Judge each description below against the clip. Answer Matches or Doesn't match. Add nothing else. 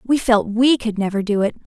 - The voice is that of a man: Doesn't match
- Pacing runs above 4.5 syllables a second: Matches